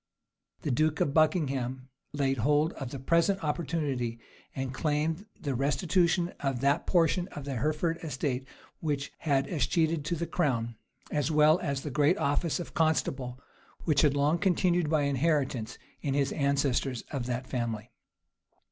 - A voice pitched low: No, medium, 145 Hz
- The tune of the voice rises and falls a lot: No, average, 3.3 semitones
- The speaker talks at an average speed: Yes, average, 155 wpm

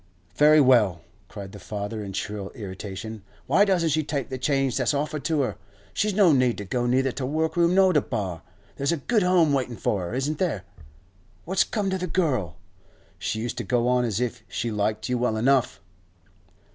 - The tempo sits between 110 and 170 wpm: No, average, 195 wpm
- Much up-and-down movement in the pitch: Yes, wide, 6.3 semitones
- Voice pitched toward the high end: No, low, 130 Hz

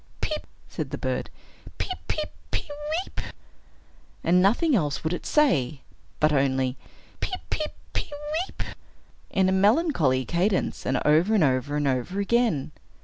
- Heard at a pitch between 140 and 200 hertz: Yes, medium, 185 Hz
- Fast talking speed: No, average, 145 wpm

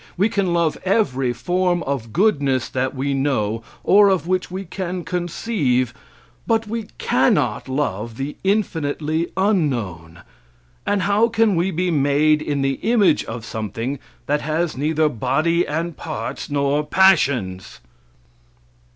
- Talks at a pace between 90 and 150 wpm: Yes, slow, 135 wpm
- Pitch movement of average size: No, wide, 5.7 semitones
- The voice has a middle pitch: Yes, medium, 155 Hz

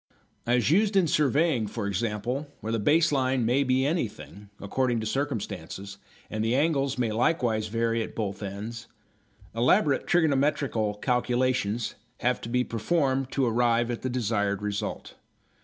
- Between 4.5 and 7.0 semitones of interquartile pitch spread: No, average, 3.9 semitones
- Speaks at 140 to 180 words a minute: Yes, average, 145 wpm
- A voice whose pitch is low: Yes, low, 120 Hz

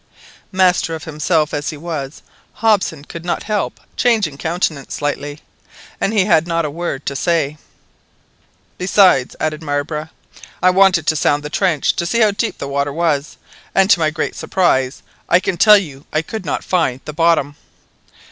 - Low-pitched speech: No, medium, 160 Hz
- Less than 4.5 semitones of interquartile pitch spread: Yes, average, 3.9 semitones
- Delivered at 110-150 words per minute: No, average, 170 wpm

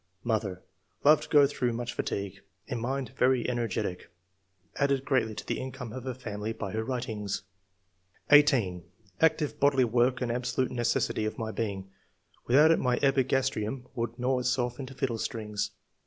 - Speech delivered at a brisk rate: No, average, 160 wpm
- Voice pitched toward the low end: Yes, low, 125 Hz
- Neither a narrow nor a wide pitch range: Yes, average, 3.1 semitones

